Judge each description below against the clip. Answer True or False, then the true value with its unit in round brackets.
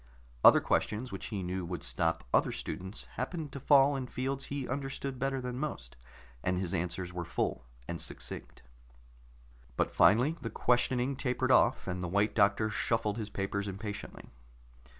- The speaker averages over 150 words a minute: True (160 wpm)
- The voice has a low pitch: True (110 Hz)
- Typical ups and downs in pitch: False (5.8 semitones)